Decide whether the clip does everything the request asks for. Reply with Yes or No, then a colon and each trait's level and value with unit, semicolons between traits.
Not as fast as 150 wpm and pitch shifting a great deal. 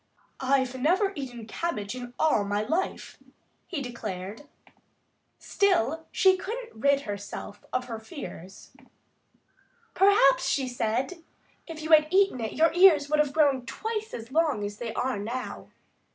Yes: average, 140 wpm; wide, 6.3 semitones